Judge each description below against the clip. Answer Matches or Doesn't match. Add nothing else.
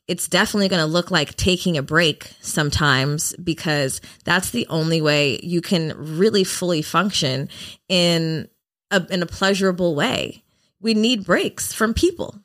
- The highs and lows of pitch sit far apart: Doesn't match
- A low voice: Doesn't match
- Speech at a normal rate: Matches